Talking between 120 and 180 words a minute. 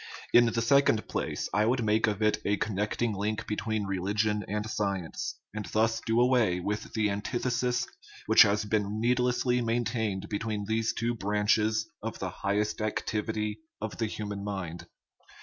Yes: average, 165 wpm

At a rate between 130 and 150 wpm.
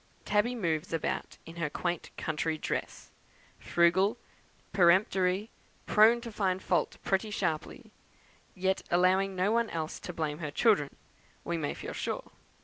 Yes: average, 140 wpm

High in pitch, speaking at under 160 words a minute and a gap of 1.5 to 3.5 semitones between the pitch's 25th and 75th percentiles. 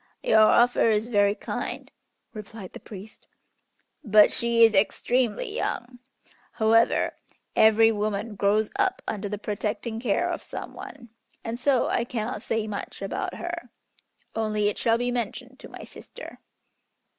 Yes: high, 225 Hz; average, 145 wpm; narrow, 2.5 semitones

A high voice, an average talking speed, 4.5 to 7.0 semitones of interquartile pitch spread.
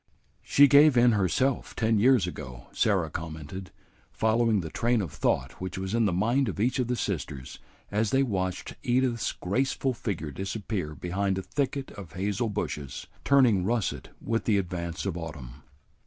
No: low, 100 Hz; average, 165 wpm; average, 5.1 semitones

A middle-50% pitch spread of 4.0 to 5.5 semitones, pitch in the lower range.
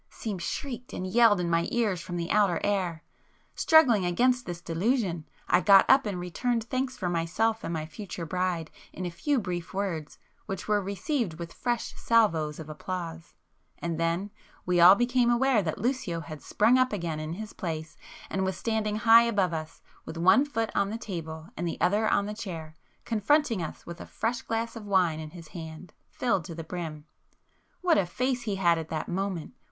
No: average, 5.2 semitones; medium, 185 Hz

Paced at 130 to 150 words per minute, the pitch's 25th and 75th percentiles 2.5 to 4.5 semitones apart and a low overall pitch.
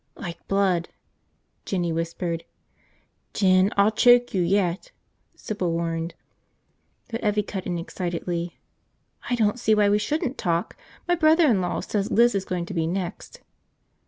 No: average, 145 wpm; average, 3.9 semitones; high, 190 Hz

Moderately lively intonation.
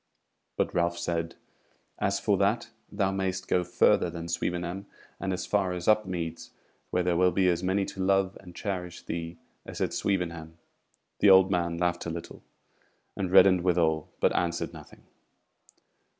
No: narrow, 1.9 semitones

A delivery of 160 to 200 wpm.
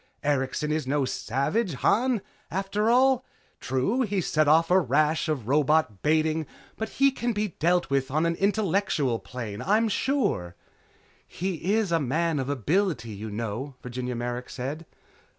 No: average, 150 wpm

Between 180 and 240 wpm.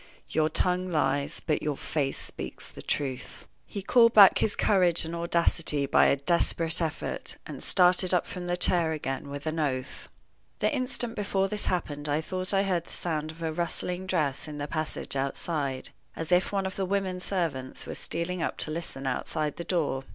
Yes: average, 190 wpm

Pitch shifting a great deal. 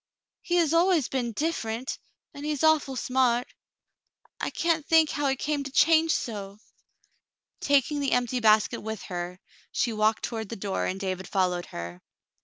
Yes: wide, 5.9 semitones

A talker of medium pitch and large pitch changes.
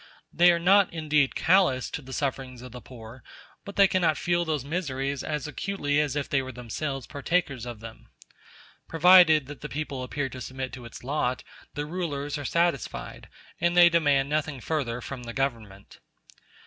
No: medium, 145 Hz; average, 4.1 semitones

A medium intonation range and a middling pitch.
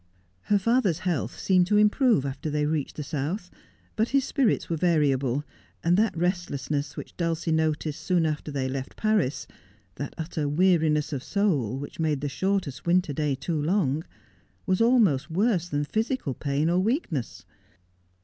Yes: average, 4.8 semitones; medium, 160 Hz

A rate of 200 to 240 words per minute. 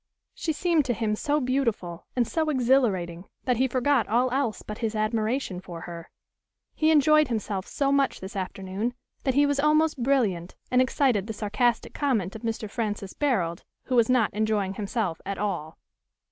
No: average, 175 wpm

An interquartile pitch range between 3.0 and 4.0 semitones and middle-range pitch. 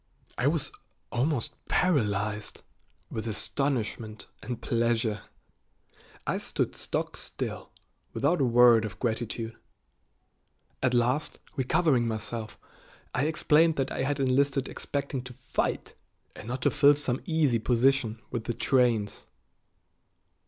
No: average, 3.5 semitones; low, 125 Hz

